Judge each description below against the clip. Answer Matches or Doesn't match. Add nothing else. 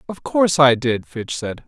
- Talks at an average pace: Doesn't match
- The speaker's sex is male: Matches